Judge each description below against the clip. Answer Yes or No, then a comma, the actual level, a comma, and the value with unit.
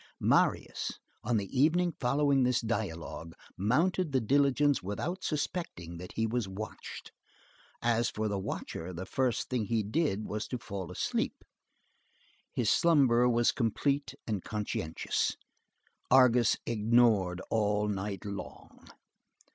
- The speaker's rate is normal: No, slow, 125 wpm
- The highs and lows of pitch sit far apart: No, average, 4.6 semitones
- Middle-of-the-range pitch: No, low, 115 Hz